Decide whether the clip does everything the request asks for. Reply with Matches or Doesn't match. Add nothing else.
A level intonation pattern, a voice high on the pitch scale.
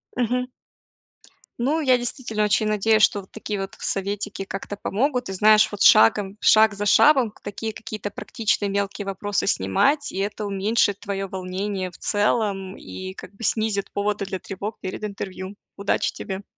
Matches